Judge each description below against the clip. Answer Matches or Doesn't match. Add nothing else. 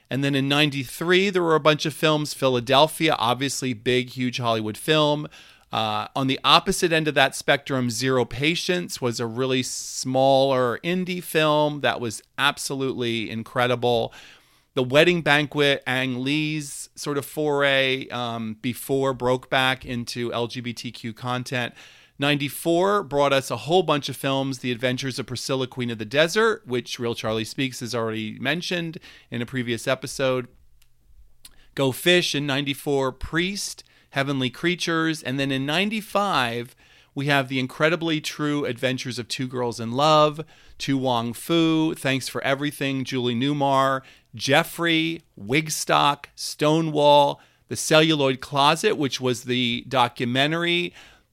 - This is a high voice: Doesn't match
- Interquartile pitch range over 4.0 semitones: Doesn't match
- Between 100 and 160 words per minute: Matches